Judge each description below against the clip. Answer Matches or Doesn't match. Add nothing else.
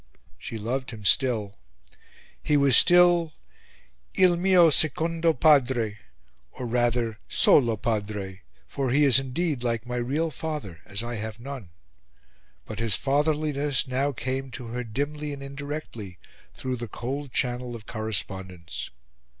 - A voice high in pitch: Doesn't match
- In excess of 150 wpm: Doesn't match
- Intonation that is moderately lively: Matches